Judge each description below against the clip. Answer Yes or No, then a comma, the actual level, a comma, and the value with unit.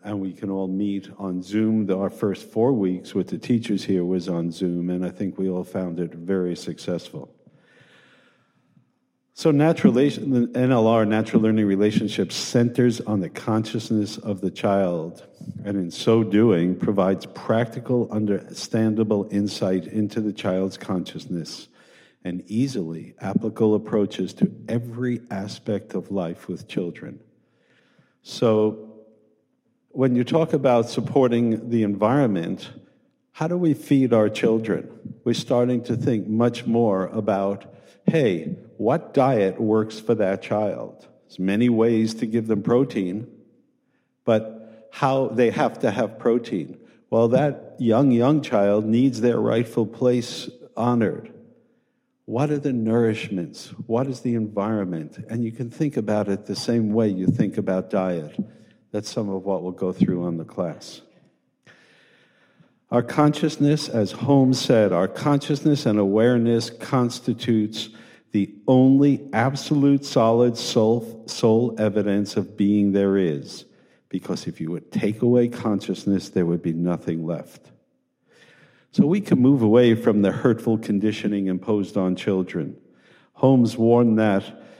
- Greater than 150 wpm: No, average, 140 wpm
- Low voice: Yes, low, 110 Hz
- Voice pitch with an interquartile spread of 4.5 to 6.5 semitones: No, average, 3.5 semitones